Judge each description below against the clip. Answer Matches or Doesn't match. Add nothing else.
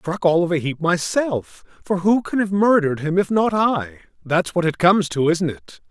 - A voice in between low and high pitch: Matches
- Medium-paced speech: Doesn't match